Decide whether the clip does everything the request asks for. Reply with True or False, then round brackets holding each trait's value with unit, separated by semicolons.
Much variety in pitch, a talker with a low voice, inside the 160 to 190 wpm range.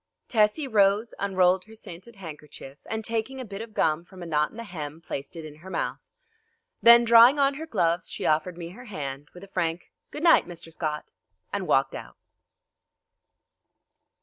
False (5.7 semitones; 185 Hz; 180 wpm)